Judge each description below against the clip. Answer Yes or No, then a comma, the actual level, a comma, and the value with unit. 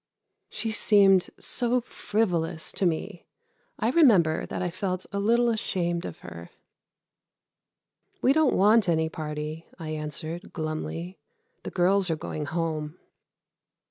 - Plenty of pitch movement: No, average, 4.8 semitones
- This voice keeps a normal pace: No, slow, 125 wpm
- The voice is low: No, medium, 175 Hz